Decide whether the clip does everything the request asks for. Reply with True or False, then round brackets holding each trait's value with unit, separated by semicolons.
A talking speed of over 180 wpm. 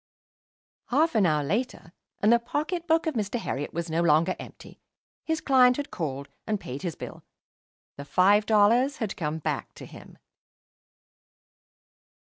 False (150 wpm)